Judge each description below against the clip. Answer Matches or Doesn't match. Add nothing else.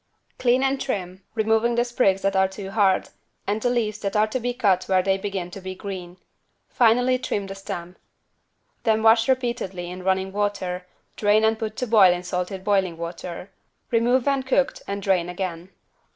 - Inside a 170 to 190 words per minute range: Matches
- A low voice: Doesn't match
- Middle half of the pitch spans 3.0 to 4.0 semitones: Matches